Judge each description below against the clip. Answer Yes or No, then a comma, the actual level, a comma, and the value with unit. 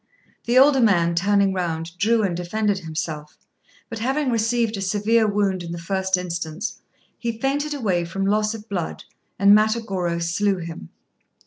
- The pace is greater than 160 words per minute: No, average, 155 wpm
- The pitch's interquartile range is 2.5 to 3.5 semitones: No, average, 4.5 semitones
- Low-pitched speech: No, high, 200 Hz